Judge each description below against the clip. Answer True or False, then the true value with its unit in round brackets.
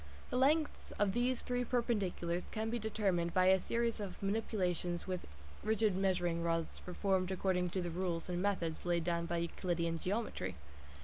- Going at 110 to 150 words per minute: False (165 wpm)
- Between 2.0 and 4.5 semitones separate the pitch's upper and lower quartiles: True (4.0 semitones)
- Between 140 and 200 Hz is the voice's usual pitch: True (185 Hz)